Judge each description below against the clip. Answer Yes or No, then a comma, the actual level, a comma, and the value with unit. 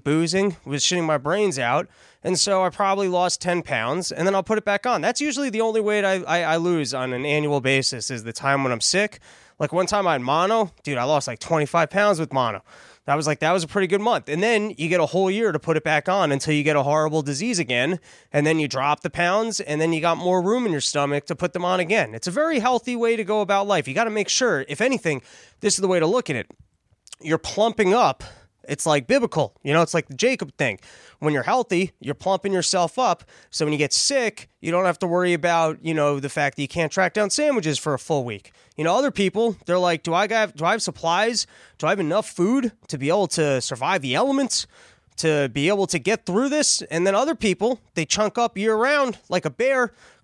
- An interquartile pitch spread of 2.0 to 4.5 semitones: No, wide, 5.6 semitones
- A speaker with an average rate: No, fast, 250 wpm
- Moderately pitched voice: Yes, medium, 175 Hz